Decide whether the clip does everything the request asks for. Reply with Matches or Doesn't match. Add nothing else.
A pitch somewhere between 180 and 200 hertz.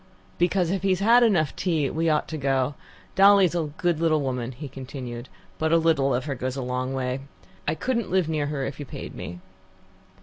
Doesn't match